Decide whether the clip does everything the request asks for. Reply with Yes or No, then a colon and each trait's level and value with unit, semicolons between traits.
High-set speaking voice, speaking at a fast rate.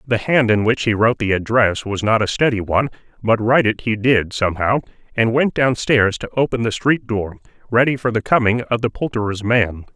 No: low, 115 Hz; fast, 210 wpm